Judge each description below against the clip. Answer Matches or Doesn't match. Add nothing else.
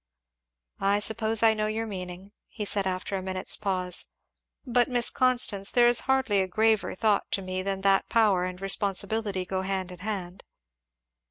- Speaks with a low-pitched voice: Doesn't match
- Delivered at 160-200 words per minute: Matches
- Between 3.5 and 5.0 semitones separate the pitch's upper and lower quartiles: Doesn't match